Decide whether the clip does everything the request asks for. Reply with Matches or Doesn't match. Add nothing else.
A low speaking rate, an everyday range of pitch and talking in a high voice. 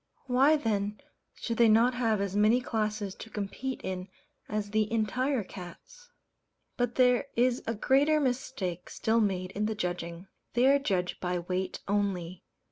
Doesn't match